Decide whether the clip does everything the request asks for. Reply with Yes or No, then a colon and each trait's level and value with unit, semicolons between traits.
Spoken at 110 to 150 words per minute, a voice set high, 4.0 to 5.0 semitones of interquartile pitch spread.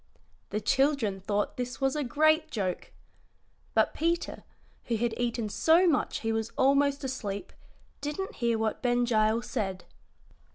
Yes: average, 140 wpm; high, 245 Hz; average, 4.5 semitones